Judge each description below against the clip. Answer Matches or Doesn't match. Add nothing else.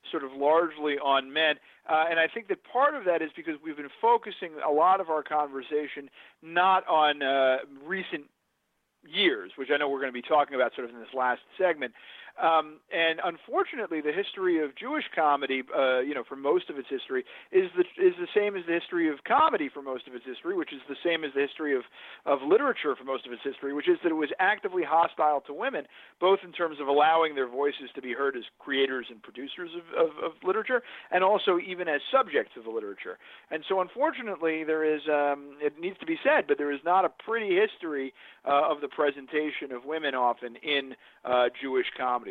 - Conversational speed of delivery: Doesn't match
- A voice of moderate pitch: Matches